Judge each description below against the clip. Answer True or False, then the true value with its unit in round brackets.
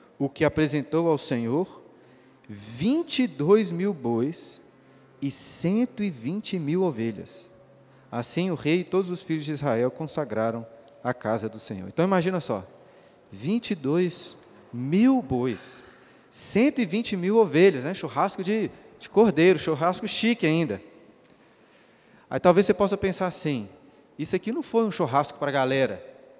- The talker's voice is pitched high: False (160 Hz)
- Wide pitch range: True (6.6 semitones)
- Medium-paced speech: True (130 wpm)